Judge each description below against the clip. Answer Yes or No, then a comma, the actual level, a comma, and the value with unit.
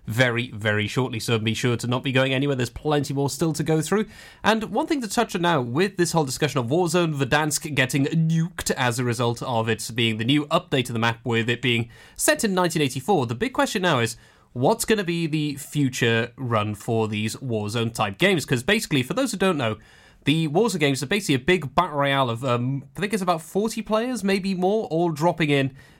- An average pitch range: No, wide, 6.8 semitones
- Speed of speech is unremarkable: No, fast, 225 wpm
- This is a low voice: No, medium, 145 Hz